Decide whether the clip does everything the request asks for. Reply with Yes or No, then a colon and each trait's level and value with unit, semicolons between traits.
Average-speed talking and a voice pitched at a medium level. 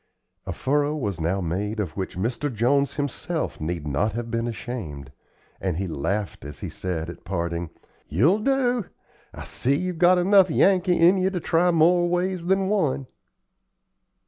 No: average, 165 wpm; low, 130 Hz